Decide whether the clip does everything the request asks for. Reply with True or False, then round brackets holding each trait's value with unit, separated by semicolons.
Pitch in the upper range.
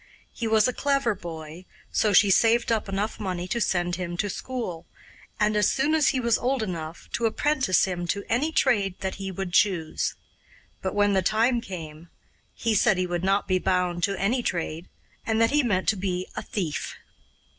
True (195 Hz)